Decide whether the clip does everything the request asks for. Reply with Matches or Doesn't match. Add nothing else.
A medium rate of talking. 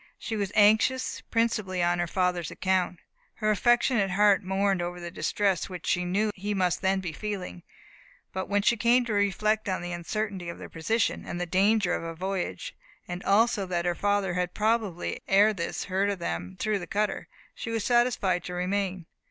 Matches